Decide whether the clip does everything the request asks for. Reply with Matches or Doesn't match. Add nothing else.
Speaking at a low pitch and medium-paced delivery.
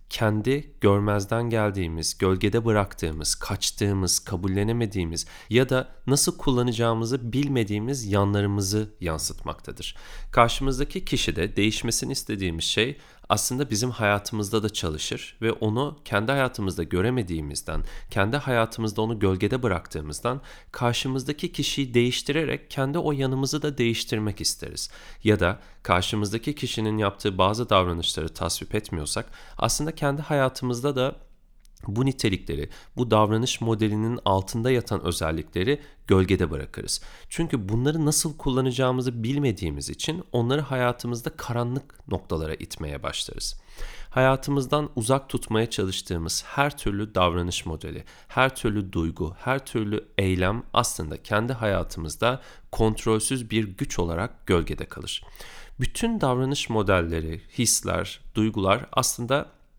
Matches